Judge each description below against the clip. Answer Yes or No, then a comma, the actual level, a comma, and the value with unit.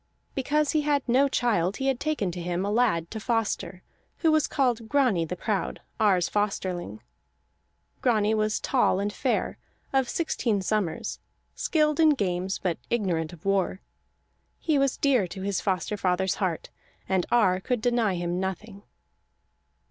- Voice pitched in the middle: No, high, 210 Hz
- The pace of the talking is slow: No, average, 155 wpm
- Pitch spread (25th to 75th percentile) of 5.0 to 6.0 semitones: Yes, wide, 5.5 semitones